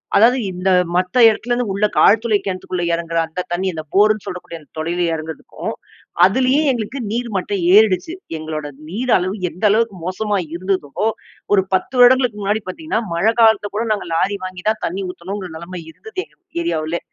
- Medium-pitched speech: No, high, 195 Hz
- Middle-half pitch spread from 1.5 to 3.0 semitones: No, average, 3.8 semitones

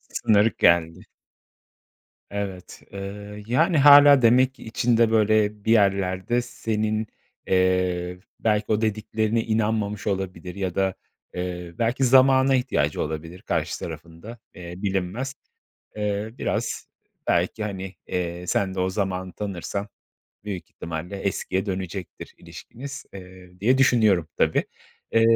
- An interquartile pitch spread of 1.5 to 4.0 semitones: Yes, average, 3.5 semitones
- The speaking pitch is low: Yes, low, 100 Hz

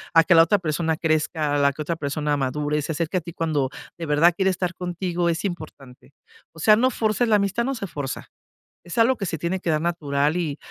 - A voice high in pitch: No, medium, 165 Hz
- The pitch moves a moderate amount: Yes, average, 3.4 semitones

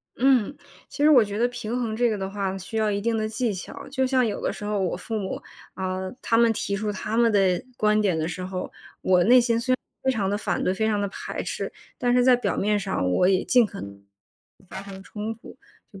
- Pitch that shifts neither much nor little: Yes, average, 3.6 semitones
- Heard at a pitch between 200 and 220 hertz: Yes, high, 210 Hz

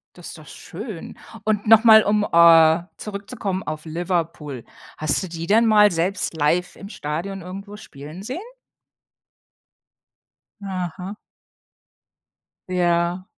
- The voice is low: No, medium, 180 Hz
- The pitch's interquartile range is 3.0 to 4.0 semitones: Yes, average, 3.6 semitones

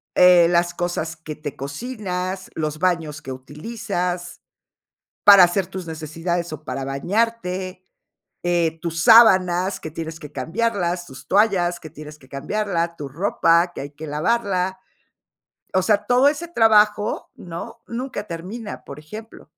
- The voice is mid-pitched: Yes, medium, 175 Hz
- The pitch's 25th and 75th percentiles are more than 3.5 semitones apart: Yes, average, 4.4 semitones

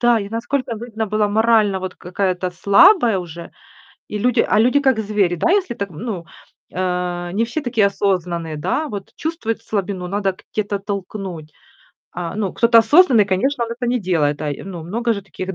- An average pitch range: Yes, average, 4.2 semitones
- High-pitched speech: Yes, high, 205 Hz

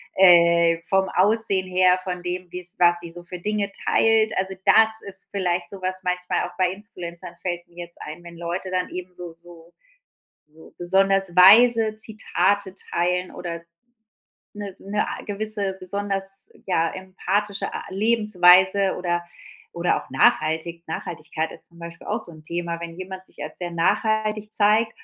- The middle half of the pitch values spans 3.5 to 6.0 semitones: No, narrow, 2.6 semitones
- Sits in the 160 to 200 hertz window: Yes, medium, 185 Hz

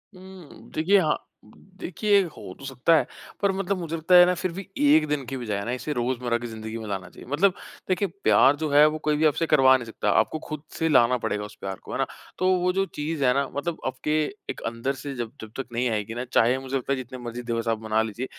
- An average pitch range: No, wide, 5.9 semitones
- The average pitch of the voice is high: No, low, 135 Hz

